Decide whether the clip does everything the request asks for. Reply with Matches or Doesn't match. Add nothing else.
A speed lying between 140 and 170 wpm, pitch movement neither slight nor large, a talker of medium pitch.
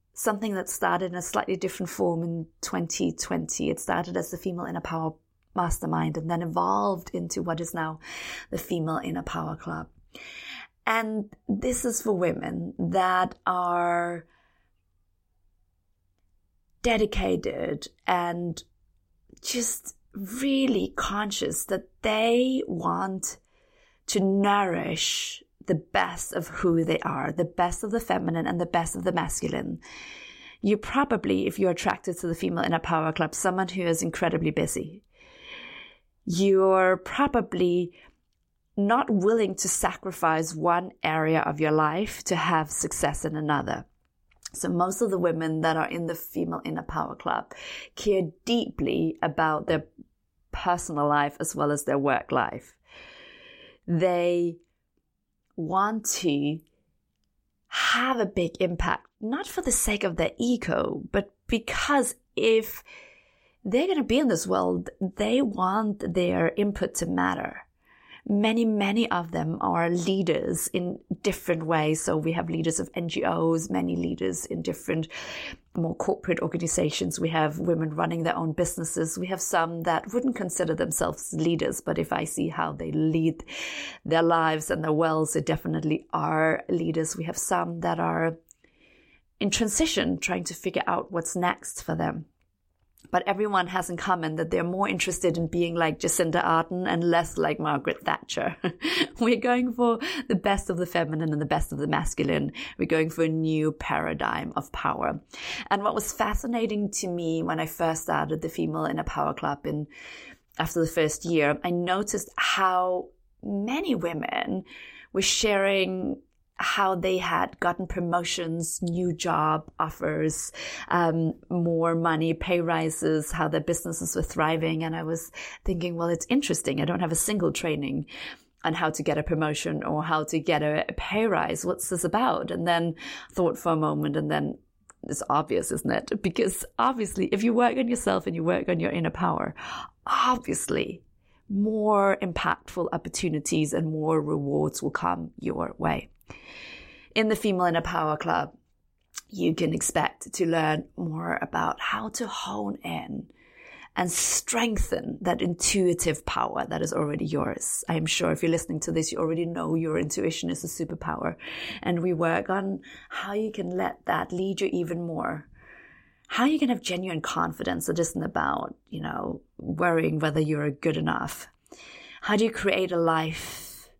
Matches